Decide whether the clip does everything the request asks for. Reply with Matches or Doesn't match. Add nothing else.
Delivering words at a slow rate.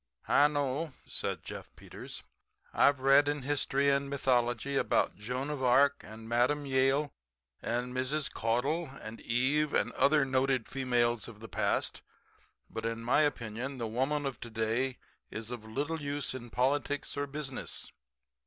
Doesn't match